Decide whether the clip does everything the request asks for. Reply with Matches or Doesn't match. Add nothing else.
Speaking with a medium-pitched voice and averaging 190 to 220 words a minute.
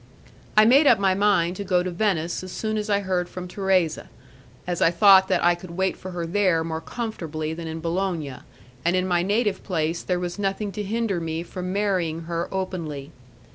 Matches